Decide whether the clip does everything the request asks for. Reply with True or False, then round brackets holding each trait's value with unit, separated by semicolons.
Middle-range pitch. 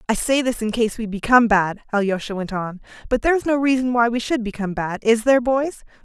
False (230 Hz)